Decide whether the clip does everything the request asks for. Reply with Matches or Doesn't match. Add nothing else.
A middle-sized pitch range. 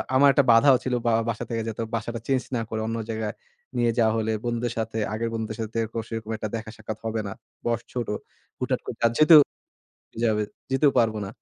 Doesn't match